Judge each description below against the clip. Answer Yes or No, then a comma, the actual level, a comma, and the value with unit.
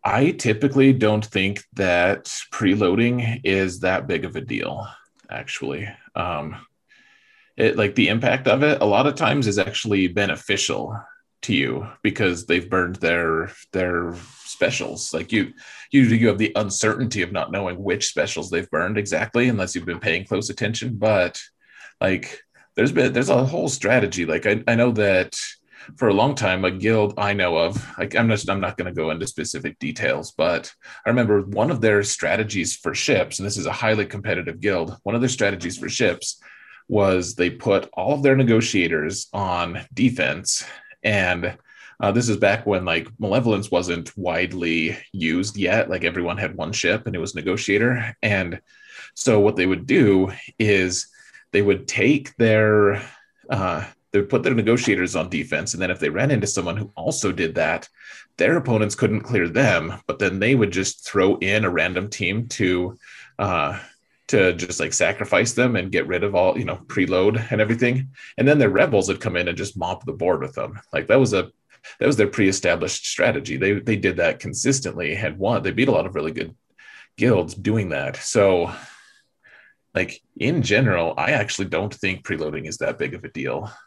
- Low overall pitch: Yes, low, 105 Hz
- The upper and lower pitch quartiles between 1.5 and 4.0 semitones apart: Yes, average, 3.6 semitones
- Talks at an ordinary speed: Yes, average, 185 wpm